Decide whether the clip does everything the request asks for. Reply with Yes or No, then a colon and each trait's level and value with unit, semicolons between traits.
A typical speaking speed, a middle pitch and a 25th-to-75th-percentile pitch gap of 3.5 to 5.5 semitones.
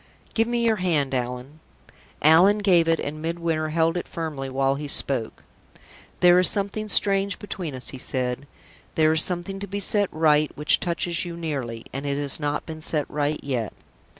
Yes: average, 180 wpm; medium, 160 Hz; average, 4.2 semitones